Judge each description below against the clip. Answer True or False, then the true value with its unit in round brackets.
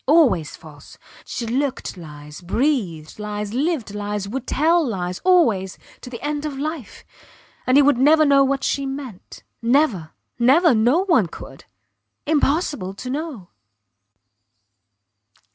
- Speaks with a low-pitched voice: False (255 Hz)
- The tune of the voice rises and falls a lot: True (6.7 semitones)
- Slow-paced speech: True (130 wpm)